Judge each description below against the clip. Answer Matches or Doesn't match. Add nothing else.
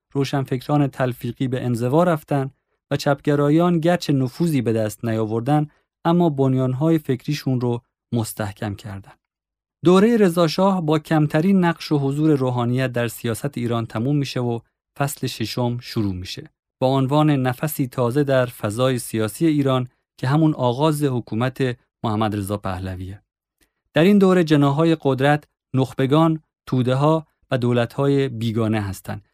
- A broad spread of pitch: Doesn't match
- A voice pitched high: Doesn't match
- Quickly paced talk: Doesn't match